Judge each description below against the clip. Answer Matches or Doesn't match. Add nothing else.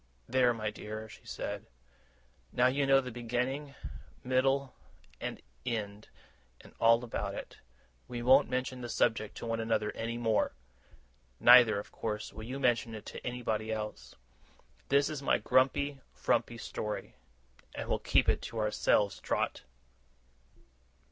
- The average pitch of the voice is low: Matches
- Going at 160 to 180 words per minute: Doesn't match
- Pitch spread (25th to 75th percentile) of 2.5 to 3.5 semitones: Matches